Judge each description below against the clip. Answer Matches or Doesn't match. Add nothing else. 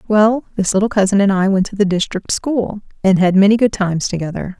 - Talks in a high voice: Matches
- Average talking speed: Doesn't match